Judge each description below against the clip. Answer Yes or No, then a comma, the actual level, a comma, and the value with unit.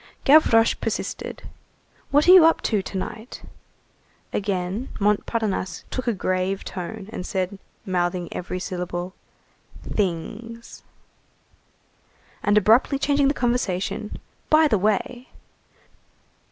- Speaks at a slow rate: Yes, slow, 105 wpm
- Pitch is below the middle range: No, high, 210 Hz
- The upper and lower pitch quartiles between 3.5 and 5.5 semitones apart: Yes, average, 4.6 semitones